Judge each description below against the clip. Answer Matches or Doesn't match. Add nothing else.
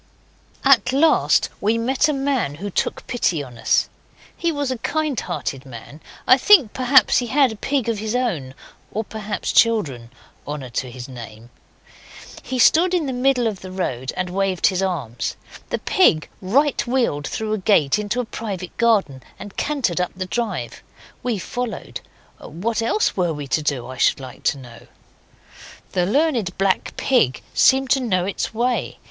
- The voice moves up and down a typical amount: Doesn't match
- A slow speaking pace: Doesn't match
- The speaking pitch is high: Matches